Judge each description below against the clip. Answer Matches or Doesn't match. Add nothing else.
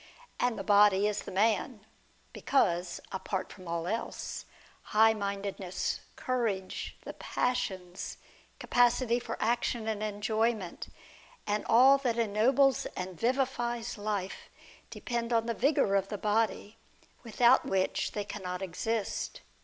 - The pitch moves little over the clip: Doesn't match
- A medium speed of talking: Doesn't match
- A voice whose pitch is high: Matches